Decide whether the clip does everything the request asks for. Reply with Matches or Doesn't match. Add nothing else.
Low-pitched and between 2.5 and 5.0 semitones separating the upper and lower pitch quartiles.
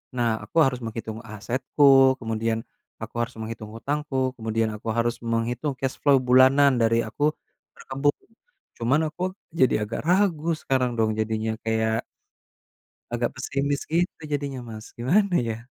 Matches